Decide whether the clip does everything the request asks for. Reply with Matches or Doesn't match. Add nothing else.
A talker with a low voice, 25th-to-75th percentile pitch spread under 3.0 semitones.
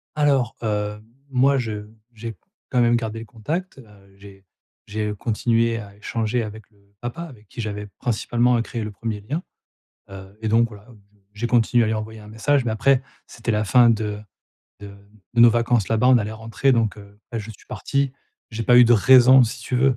Matches